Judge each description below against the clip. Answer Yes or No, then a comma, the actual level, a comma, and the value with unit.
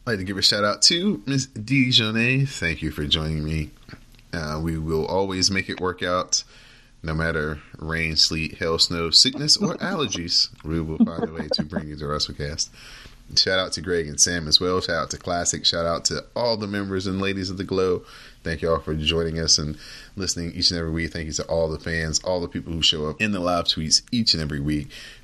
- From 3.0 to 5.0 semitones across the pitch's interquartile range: Yes, average, 3.7 semitones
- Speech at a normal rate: No, fast, 235 wpm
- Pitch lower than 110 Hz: Yes, very low, 85 Hz